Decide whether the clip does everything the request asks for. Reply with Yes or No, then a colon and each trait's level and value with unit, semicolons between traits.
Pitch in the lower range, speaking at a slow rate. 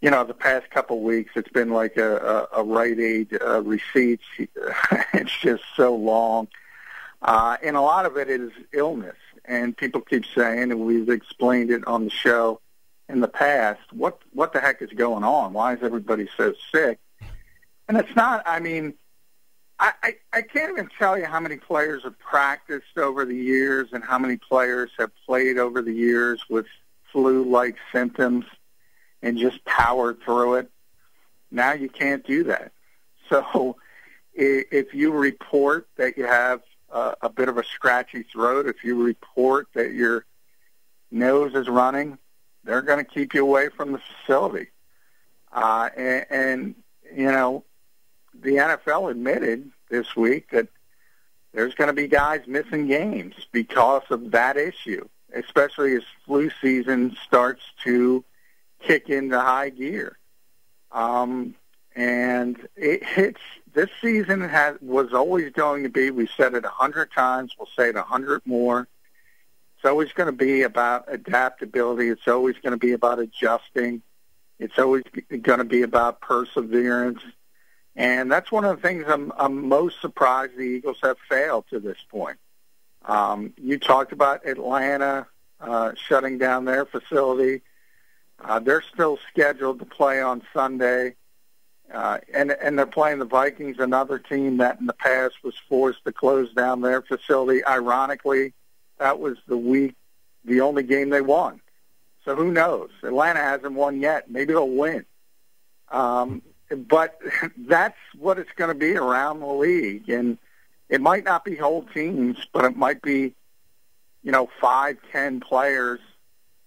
No: low, 130 Hz; average, 160 wpm